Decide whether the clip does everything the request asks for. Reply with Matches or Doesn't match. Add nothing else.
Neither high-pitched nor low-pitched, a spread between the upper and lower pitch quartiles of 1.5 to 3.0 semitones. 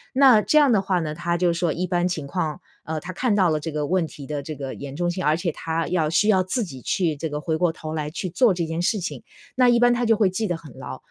Doesn't match